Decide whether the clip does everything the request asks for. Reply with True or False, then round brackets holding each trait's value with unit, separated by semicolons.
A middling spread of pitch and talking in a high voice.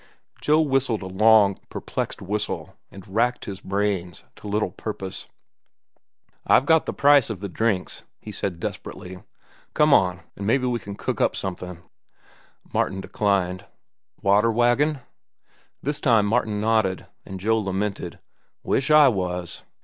False (4.1 semitones; 105 Hz)